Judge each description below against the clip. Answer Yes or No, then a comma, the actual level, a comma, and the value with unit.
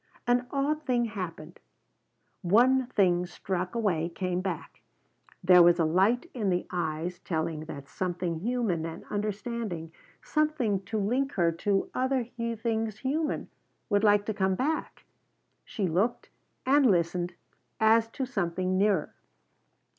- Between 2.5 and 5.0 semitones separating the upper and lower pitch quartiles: No, wide, 5.4 semitones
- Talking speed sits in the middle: No, slow, 130 wpm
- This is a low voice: No, high, 200 Hz